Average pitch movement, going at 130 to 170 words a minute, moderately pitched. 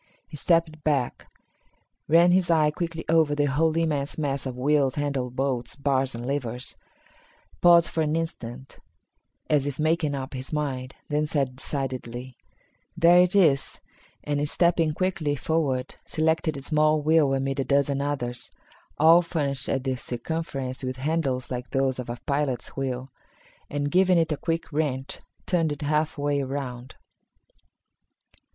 Yes: average, 3.2 semitones; average, 150 wpm; medium, 145 Hz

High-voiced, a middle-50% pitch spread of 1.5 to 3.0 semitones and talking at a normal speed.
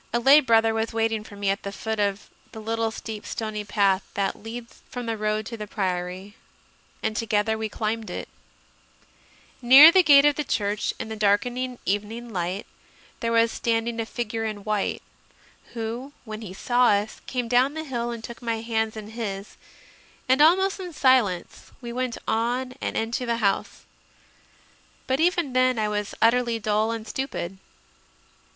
Yes: high, 225 Hz; narrow, 2.6 semitones; average, 170 wpm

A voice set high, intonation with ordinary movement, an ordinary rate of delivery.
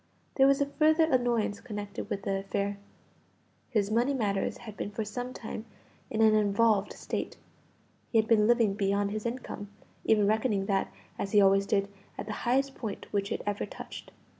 Yes: high, 215 Hz; average, 3.0 semitones; average, 180 wpm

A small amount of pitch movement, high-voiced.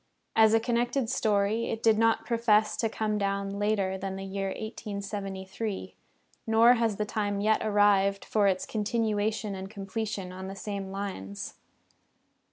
Yes: narrow, 2.1 semitones; high, 205 Hz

